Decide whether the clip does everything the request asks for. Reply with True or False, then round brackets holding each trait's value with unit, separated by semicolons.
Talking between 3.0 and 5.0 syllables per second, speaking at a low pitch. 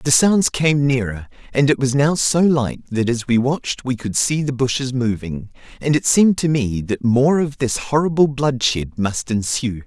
True (4.6 syllables/s; 130 Hz)